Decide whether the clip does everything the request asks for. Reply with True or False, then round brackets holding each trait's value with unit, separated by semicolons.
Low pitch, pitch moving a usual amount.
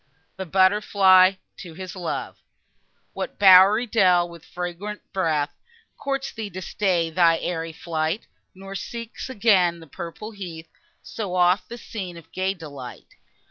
False (185 Hz; 3.1 semitones)